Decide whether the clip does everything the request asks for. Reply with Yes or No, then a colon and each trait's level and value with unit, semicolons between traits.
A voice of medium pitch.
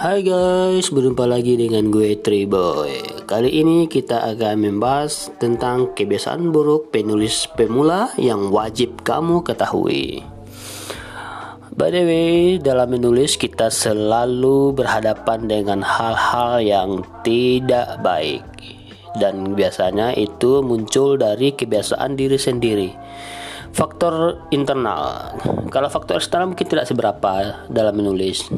No: low, 125 Hz